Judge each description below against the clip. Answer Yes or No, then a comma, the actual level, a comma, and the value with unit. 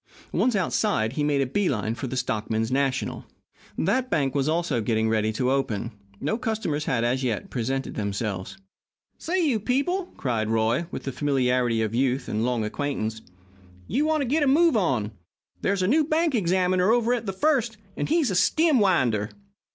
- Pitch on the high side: No, medium, 145 Hz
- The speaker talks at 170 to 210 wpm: Yes, average, 185 wpm